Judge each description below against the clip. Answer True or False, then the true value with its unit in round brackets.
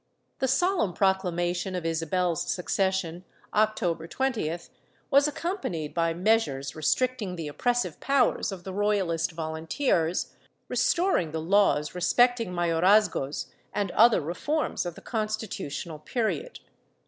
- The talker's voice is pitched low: False (185 Hz)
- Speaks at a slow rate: True (110 wpm)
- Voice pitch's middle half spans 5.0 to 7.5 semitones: True (5.3 semitones)